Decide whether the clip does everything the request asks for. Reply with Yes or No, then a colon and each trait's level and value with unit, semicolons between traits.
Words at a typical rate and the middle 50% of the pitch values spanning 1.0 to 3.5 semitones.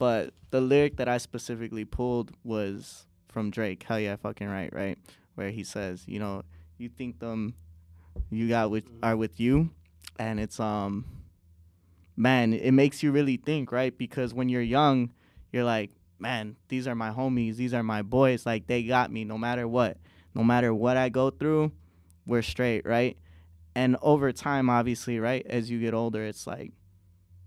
No: average, 175 wpm; average, 3.9 semitones